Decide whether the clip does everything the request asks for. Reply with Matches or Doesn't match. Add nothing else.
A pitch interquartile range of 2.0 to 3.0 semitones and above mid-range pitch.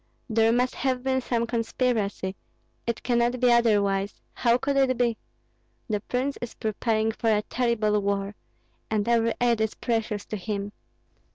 Matches